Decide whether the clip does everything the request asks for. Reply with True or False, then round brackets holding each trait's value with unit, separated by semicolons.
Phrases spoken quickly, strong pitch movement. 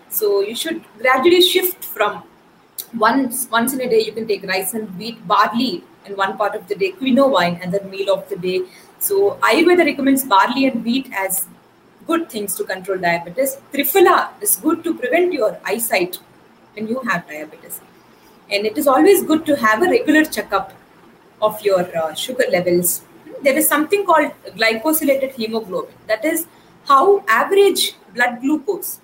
False (170 wpm; 8.1 semitones)